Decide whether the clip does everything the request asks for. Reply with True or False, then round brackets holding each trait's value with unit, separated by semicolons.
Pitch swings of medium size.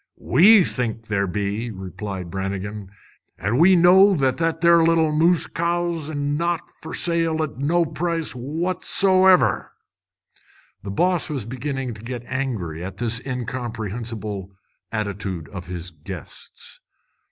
False (8.4 semitones)